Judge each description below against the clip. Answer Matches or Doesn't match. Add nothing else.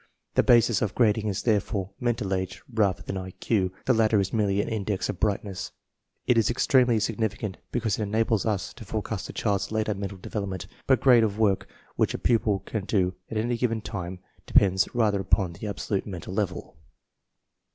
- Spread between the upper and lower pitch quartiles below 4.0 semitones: Matches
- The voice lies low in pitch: Matches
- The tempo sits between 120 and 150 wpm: Doesn't match